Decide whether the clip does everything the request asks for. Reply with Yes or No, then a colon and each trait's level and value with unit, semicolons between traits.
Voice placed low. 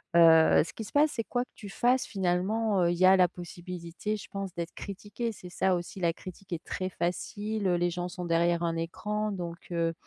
No: medium, 180 Hz